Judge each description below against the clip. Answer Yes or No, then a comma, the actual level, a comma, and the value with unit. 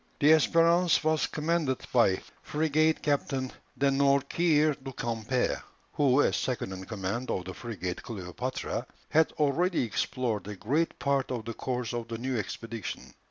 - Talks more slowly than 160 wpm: Yes, average, 150 wpm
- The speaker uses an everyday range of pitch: Yes, average, 4.8 semitones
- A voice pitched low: Yes, low, 130 Hz